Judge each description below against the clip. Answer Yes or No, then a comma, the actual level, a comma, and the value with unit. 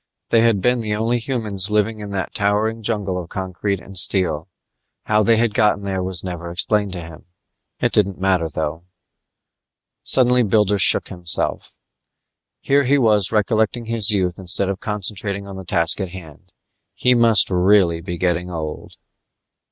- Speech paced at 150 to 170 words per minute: Yes, average, 160 wpm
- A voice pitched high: No, low, 100 Hz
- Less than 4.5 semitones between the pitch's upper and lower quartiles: Yes, average, 3.3 semitones